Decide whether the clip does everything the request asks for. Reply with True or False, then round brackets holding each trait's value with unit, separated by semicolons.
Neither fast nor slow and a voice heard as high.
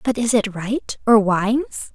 True (185 wpm; 220 Hz)